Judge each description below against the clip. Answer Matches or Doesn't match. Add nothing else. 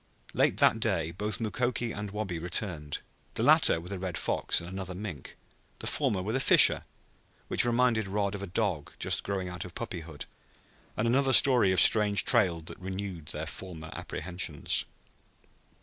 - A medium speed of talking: Matches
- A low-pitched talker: Matches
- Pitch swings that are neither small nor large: Matches